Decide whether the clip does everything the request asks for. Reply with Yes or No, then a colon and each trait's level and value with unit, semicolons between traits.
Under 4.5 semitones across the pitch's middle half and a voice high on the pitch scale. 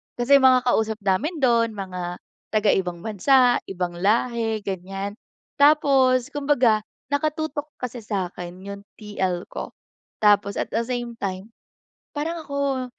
No: average, 5.3 semitones; high, 230 Hz